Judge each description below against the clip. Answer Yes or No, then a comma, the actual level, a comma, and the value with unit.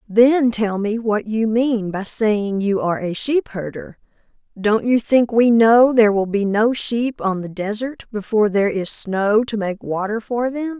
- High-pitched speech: Yes, high, 220 Hz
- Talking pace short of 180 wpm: No, average, 195 wpm